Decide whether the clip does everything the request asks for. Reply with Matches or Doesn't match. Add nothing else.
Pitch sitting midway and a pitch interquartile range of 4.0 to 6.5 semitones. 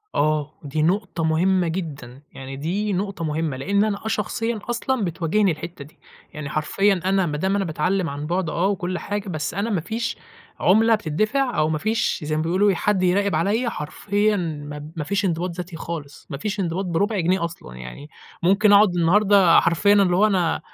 Matches